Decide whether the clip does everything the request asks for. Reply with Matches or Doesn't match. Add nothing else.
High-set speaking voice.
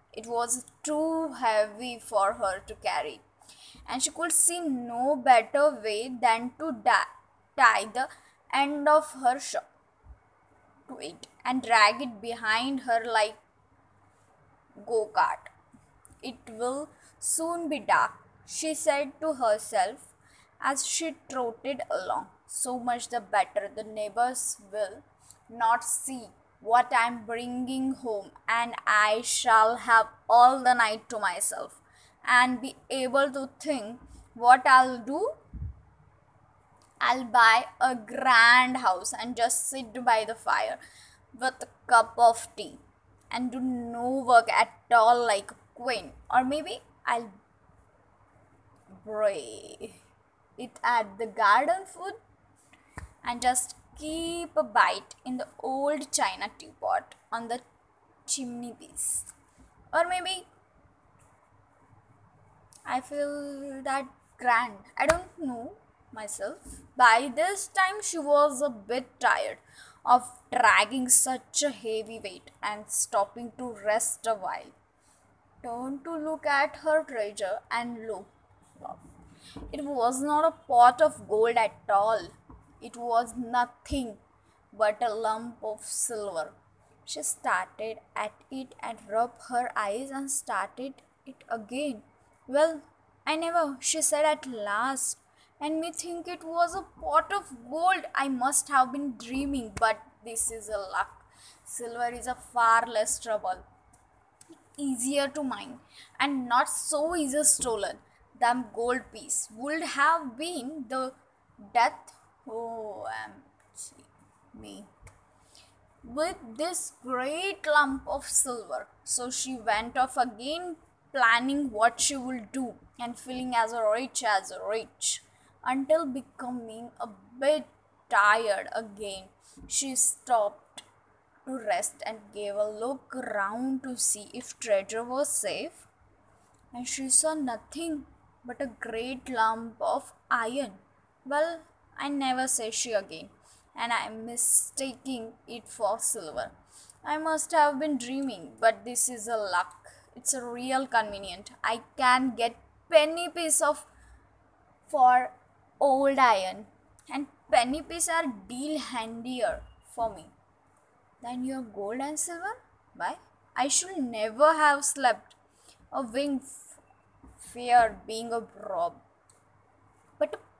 Matches